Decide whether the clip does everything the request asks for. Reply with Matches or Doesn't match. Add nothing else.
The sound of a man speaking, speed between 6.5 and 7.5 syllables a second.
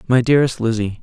Matches